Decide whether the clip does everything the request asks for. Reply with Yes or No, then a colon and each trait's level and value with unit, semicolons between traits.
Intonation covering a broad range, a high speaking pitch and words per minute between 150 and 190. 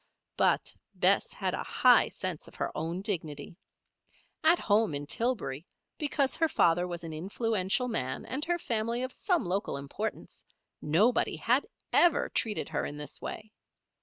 Yes: wide, 7.5 semitones; high, 205 Hz; average, 155 wpm